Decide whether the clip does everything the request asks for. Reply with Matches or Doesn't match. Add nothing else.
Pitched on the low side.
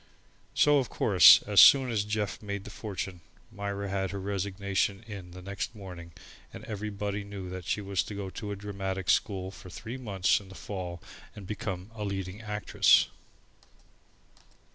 Matches